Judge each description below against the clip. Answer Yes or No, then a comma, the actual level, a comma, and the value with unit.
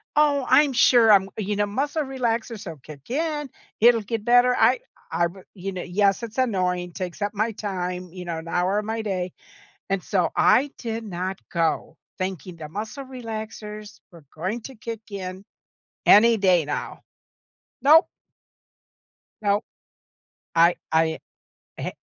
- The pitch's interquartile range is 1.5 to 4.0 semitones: No, average, 4.4 semitones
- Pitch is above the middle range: Yes, high, 205 Hz